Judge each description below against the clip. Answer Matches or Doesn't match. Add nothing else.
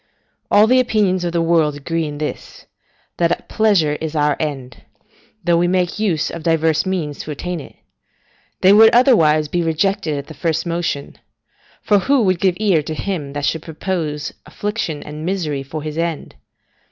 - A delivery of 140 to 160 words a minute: Doesn't match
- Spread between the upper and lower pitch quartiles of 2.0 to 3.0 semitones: Doesn't match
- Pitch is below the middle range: Doesn't match